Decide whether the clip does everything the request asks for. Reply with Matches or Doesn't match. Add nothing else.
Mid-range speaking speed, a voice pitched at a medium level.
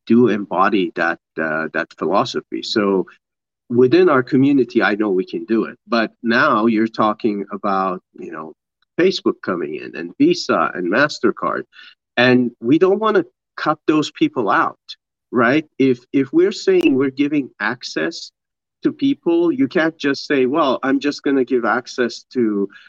Matches